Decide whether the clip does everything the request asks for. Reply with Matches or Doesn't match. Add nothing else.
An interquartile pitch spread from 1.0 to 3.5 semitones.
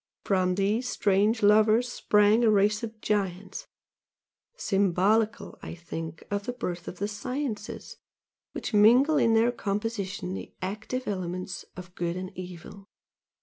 Matches